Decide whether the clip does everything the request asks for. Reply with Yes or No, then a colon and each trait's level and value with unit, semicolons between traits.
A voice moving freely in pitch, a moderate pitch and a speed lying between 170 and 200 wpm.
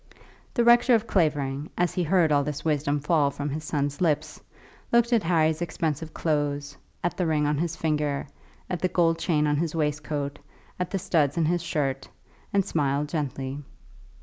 No: average, 3.0 semitones; medium, 155 Hz; average, 175 wpm